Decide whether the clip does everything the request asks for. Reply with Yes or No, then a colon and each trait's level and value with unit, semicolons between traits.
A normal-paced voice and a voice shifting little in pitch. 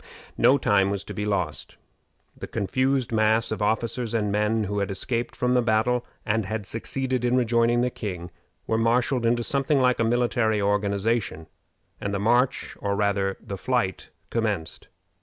No: average, 165 wpm; average, 3.2 semitones